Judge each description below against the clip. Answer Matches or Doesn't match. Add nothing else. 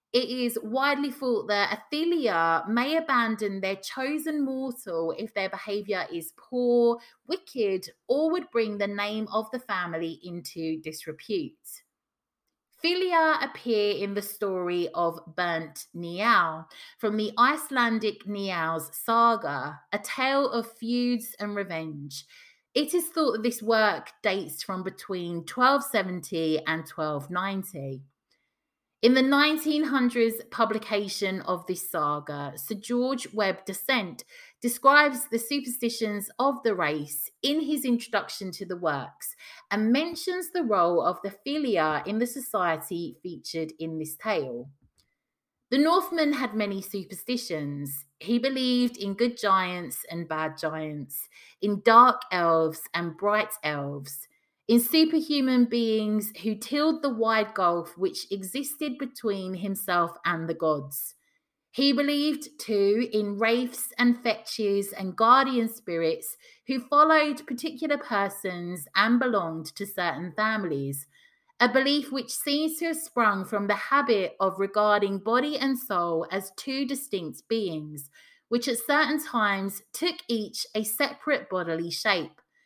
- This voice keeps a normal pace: Doesn't match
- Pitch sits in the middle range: Doesn't match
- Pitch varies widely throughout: Matches